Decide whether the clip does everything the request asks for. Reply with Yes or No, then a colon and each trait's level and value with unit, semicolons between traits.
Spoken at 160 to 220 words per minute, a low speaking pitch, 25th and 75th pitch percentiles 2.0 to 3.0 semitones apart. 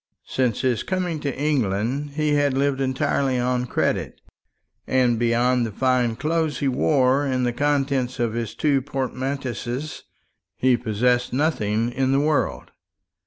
No: average, 140 wpm; low, 130 Hz; narrow, 2.6 semitones